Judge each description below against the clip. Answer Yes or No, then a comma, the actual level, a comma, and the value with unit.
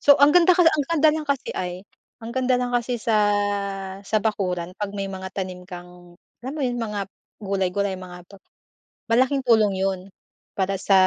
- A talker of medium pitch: No, high, 205 Hz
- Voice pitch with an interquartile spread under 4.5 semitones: No, average, 5.3 semitones